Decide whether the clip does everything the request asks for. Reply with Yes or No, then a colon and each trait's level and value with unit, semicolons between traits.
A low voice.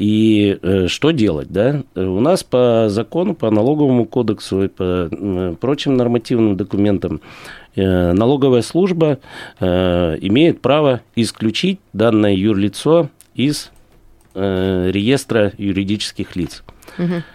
Yes: low, 110 Hz